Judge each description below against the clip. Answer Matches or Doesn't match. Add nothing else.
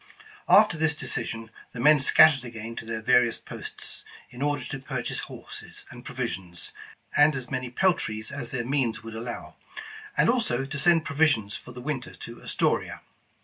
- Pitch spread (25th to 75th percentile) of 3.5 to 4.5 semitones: Matches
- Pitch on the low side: Matches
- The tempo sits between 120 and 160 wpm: Doesn't match